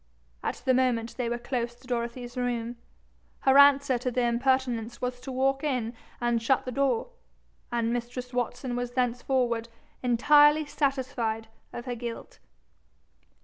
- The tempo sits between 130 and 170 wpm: Yes, average, 145 wpm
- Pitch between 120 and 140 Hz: No, high, 245 Hz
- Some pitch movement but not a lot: No, narrow, 1.7 semitones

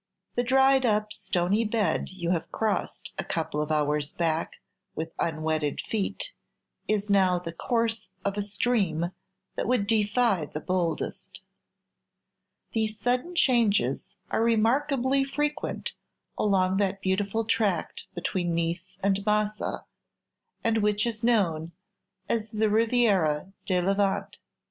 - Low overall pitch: No, high, 205 Hz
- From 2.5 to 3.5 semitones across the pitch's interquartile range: No, average, 4.6 semitones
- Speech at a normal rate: No, slow, 125 wpm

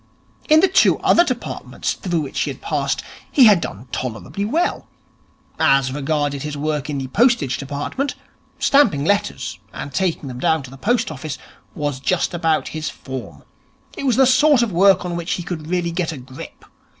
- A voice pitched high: No, medium, 160 Hz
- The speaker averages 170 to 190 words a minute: Yes, average, 185 wpm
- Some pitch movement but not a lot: No, wide, 6.6 semitones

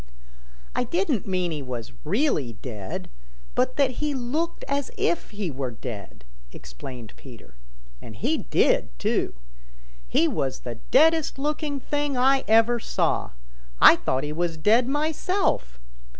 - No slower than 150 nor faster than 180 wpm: No, slow, 135 wpm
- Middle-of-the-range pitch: No, high, 225 Hz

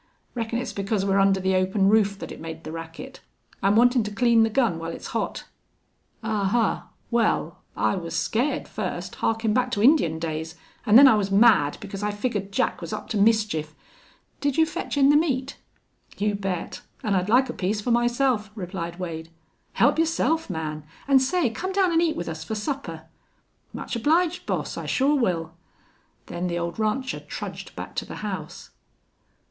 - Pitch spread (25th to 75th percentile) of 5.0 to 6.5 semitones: Yes, wide, 5.6 semitones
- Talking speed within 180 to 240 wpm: Yes, average, 185 wpm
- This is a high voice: Yes, high, 210 Hz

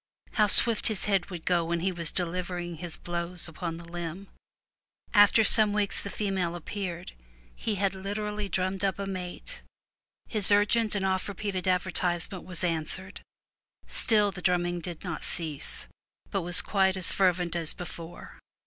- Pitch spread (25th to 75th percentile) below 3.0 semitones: Yes, narrow, 2.5 semitones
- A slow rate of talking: No, average, 160 wpm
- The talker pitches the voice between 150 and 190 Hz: Yes, medium, 185 Hz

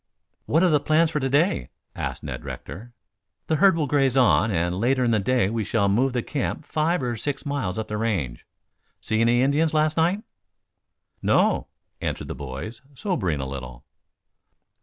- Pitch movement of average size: No, wide, 6.9 semitones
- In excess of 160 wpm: Yes, average, 180 wpm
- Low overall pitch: Yes, low, 125 Hz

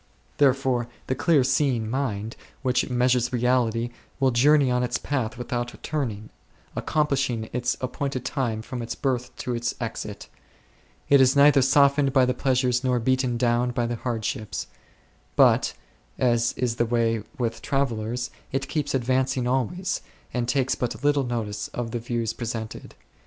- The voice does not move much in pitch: Yes, narrow, 2.1 semitones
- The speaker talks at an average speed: Yes, average, 150 wpm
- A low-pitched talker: Yes, low, 125 Hz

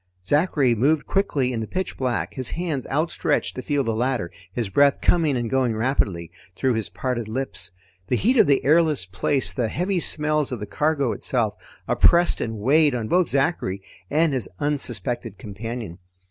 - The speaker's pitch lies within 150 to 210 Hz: No, low, 130 Hz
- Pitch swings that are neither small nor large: Yes, average, 4.9 semitones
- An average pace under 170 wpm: No, average, 175 wpm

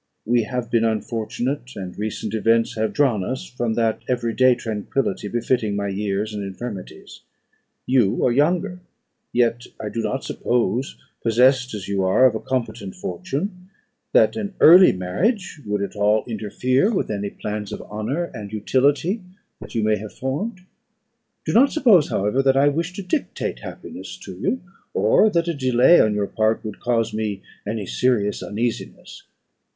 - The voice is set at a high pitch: No, low, 115 Hz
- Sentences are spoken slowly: No, average, 165 wpm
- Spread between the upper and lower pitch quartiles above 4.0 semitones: Yes, average, 4.4 semitones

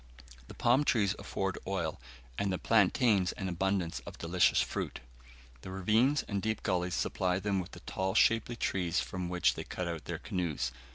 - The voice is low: Yes, very low, 95 Hz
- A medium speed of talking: Yes, average, 175 wpm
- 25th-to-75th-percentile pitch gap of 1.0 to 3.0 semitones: Yes, narrow, 2.6 semitones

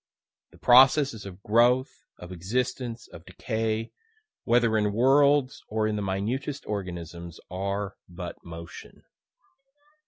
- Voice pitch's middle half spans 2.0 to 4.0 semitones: No, average, 4.7 semitones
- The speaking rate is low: Yes, slow, 115 wpm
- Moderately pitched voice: No, low, 110 Hz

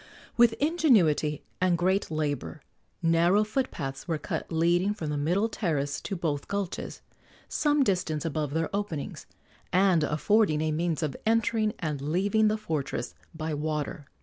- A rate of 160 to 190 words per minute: No, average, 150 wpm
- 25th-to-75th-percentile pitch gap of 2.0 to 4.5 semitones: No, average, 5.2 semitones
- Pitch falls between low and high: Yes, medium, 170 Hz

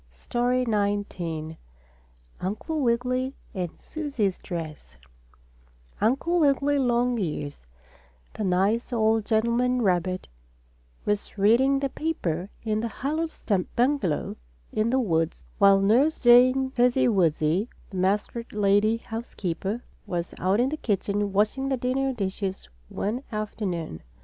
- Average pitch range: Yes, average, 4.9 semitones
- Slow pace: Yes, slow, 120 wpm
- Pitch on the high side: Yes, high, 220 Hz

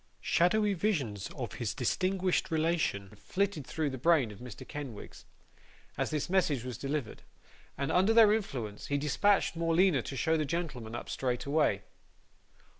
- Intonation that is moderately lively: No, wide, 6.3 semitones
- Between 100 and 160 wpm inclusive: Yes, average, 145 wpm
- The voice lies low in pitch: No, medium, 150 Hz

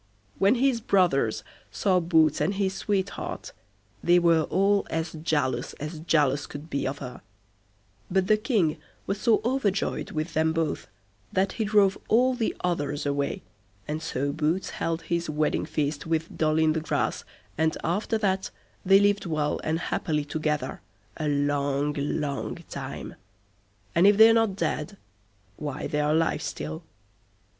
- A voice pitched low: No, medium, 160 Hz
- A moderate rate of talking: Yes, average, 150 wpm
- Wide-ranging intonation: No, average, 4.6 semitones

